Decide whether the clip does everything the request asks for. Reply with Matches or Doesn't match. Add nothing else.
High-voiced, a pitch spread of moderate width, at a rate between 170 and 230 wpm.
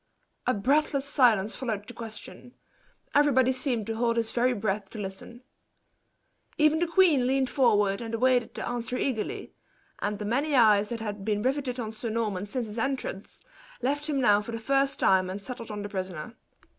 Matches